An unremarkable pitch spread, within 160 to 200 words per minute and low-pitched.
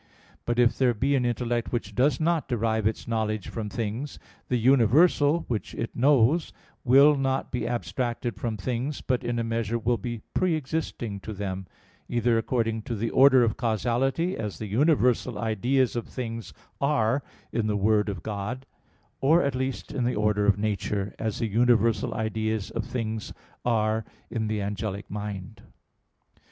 Yes: average, 3.0 semitones; average, 165 wpm; low, 115 Hz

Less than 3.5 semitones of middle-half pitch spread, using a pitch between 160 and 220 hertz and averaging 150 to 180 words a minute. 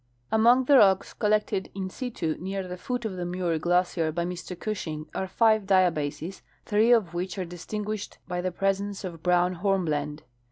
Yes: average, 2.9 semitones; medium, 185 Hz; average, 175 wpm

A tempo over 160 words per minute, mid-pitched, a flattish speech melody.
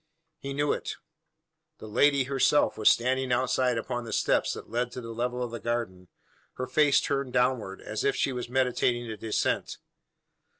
No: average, 175 wpm; low, 125 Hz; narrow, 2.0 semitones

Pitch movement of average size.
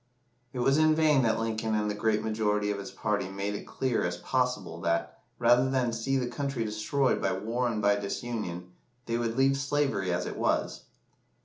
Yes: average, 4.0 semitones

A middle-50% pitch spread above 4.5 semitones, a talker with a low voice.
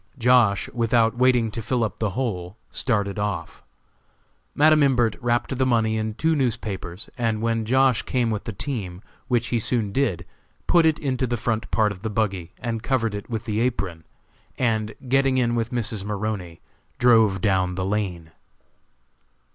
No: average, 3.3 semitones; low, 115 Hz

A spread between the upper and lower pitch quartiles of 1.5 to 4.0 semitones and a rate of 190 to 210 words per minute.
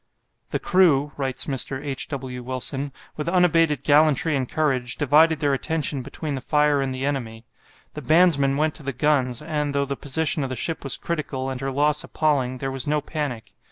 Yes: narrow, 2.4 semitones; average, 195 wpm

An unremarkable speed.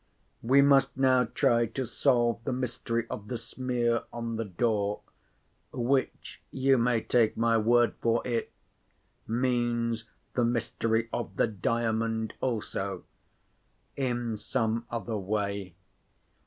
No: slow, 115 wpm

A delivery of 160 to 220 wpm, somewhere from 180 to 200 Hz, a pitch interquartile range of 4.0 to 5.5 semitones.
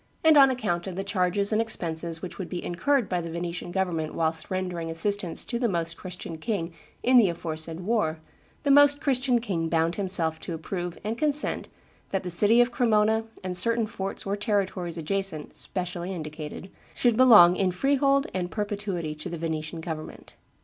Yes: average, 175 wpm; medium, 185 Hz; average, 4.7 semitones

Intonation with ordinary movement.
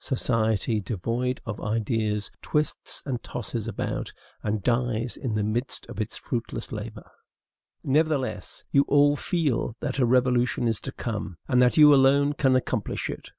Yes: average, 3.6 semitones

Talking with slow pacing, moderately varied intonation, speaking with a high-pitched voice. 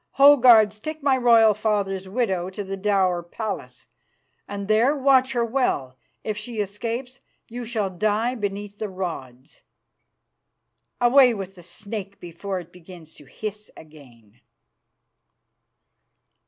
Yes: slow, 125 wpm; average, 4.3 semitones; high, 205 Hz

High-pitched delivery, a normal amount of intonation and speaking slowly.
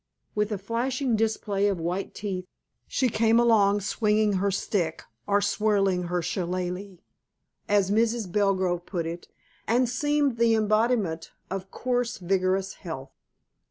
Yes: high, 205 Hz; average, 3.5 semitones; slow, 130 wpm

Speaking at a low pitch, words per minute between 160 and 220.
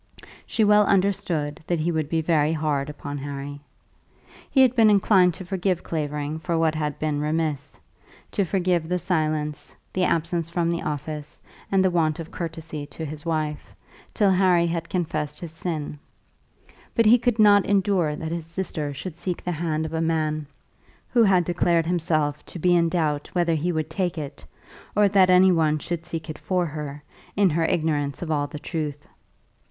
No: medium, 165 Hz; average, 180 wpm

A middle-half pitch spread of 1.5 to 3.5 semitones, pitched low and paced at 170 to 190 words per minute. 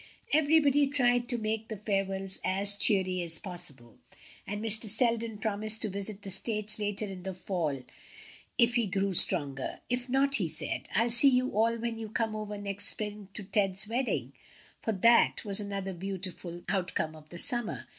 No: average, 3.2 semitones; high, 205 Hz; average, 175 wpm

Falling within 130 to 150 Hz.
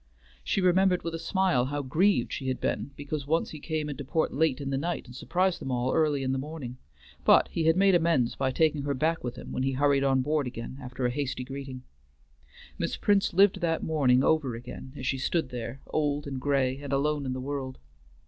Yes: medium, 140 Hz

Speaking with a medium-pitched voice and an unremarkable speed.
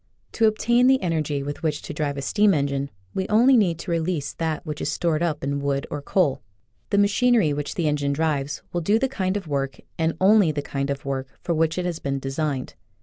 No: medium, 160 Hz; fast, 215 wpm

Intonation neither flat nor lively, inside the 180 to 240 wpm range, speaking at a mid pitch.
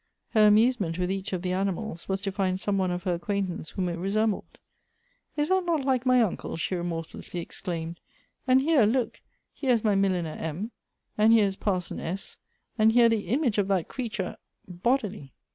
No: average, 4.4 semitones; average, 195 wpm; high, 200 Hz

